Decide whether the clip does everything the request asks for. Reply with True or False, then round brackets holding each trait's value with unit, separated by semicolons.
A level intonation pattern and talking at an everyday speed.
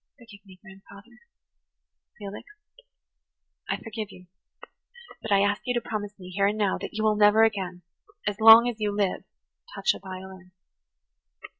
True (2.1 semitones; 155 wpm)